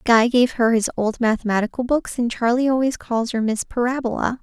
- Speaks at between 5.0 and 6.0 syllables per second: Yes, 5.4 syllables/s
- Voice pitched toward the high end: Yes, high, 240 Hz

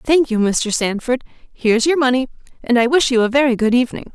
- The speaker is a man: No, female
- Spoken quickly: Yes, fast, 230 wpm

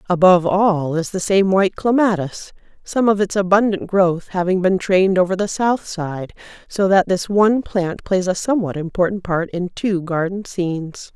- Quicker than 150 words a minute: Yes, average, 180 wpm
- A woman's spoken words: Yes, female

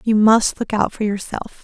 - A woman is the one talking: Yes, female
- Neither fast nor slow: No, fast, 220 wpm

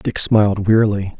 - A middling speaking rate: Yes, average, 150 wpm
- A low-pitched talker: Yes, low, 105 Hz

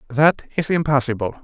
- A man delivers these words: Yes, male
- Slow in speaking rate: Yes, slow, 125 wpm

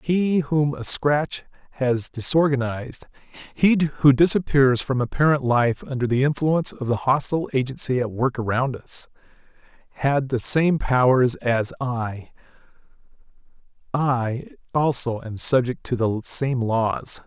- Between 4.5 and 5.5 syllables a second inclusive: No, 4.2 syllables/s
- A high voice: No, low, 130 Hz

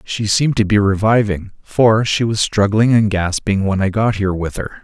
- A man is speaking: Yes, male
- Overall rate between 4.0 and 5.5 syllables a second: Yes, 5.1 syllables/s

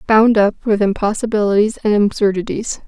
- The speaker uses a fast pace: No, slow, 125 wpm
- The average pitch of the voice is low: No, high, 210 Hz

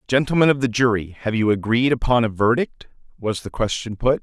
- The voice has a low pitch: Yes, low, 120 Hz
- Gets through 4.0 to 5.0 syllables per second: No, 5.6 syllables/s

